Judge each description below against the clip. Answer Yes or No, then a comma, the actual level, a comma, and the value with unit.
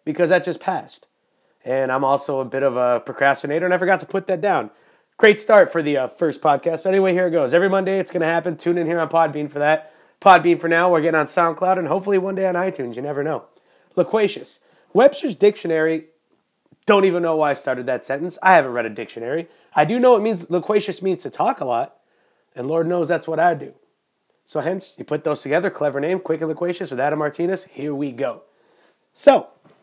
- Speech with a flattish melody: No, average, 4.0 semitones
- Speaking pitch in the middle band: Yes, medium, 170 Hz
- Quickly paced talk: Yes, fast, 225 wpm